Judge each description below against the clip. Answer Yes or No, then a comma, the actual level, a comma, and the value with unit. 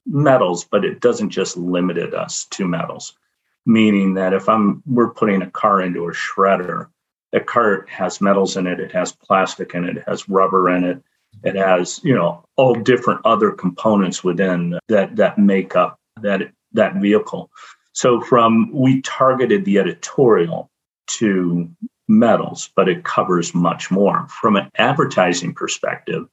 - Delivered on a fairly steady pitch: No, average, 3.8 semitones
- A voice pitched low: Yes, very low, 95 Hz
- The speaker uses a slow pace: No, average, 155 wpm